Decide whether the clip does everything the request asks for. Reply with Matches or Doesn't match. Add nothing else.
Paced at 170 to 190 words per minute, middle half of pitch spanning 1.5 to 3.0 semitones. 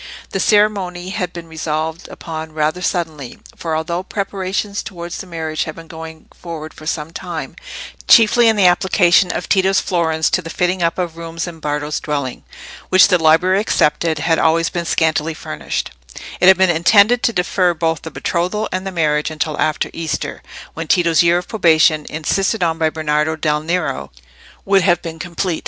Matches